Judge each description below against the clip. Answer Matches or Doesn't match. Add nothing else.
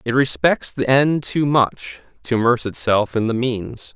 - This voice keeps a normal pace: Matches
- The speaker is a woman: Doesn't match